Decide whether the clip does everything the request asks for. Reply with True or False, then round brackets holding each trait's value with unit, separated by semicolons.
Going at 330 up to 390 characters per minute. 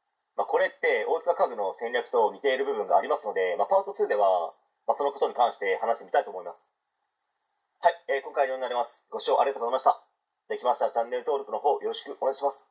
False (470 characters per minute)